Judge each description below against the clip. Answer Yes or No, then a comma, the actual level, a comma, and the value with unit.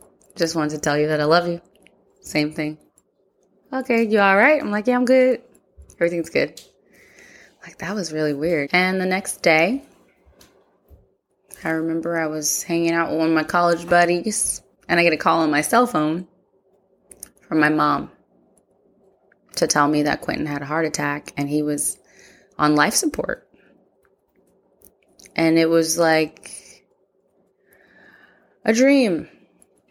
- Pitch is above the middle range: No, medium, 170 Hz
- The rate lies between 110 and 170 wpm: Yes, average, 150 wpm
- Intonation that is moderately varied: Yes, average, 4.0 semitones